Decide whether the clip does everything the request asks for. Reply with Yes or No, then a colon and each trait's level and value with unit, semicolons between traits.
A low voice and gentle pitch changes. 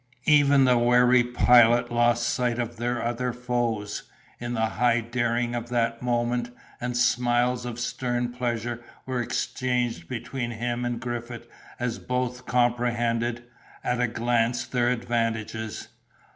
Yes: low, 120 Hz; narrow, 0.7 semitones